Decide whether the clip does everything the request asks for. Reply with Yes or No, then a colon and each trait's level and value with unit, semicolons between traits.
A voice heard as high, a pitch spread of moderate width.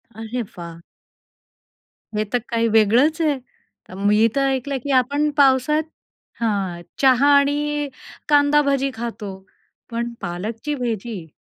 Yes: high, 245 Hz; average, 4.6 semitones